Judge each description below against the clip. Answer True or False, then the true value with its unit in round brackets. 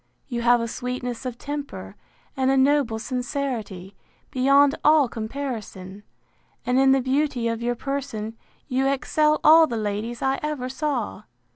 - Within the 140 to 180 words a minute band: True (145 wpm)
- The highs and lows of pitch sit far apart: False (3.2 semitones)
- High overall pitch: True (255 Hz)